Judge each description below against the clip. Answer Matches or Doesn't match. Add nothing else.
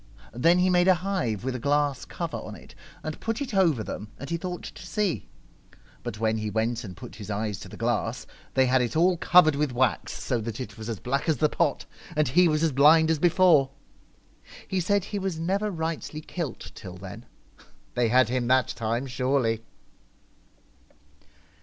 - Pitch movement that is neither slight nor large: Doesn't match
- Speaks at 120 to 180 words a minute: Doesn't match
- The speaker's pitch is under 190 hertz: Matches